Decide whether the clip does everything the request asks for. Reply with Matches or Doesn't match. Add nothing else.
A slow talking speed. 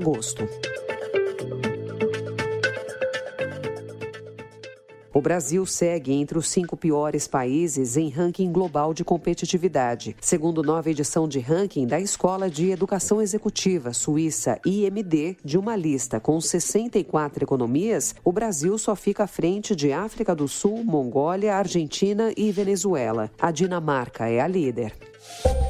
Matches